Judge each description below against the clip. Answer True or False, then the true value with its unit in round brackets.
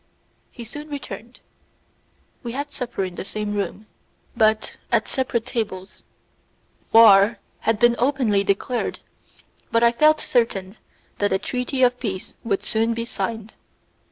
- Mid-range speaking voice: False (230 Hz)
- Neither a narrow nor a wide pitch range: True (3.2 semitones)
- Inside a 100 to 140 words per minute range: True (135 wpm)